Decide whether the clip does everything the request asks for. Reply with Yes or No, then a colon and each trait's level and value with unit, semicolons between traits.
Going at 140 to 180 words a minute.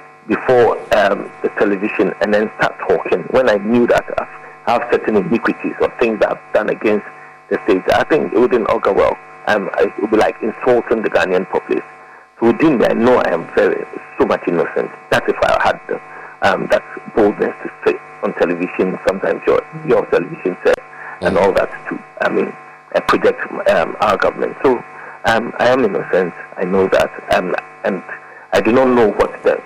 No: average, 190 wpm